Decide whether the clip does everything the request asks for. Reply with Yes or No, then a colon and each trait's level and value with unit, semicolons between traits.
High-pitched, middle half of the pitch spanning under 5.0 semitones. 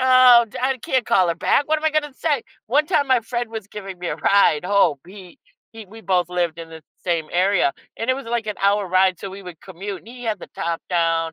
No: high, 200 Hz; average, 5.3 semitones